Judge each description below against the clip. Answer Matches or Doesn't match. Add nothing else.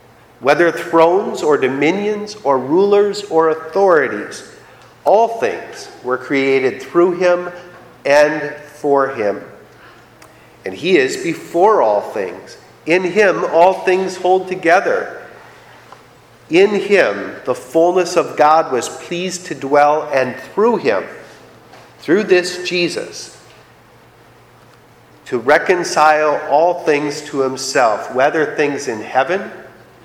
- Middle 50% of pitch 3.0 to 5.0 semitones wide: Matches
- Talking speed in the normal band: Doesn't match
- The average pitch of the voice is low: Doesn't match